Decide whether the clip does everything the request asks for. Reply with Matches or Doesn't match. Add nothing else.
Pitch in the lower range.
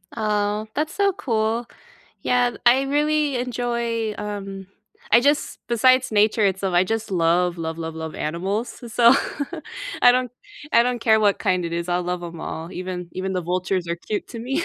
Doesn't match